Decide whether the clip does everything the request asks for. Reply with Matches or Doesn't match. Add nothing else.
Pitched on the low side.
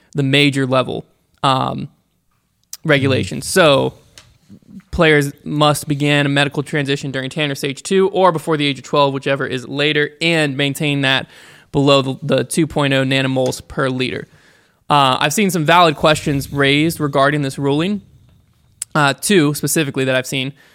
Doesn't match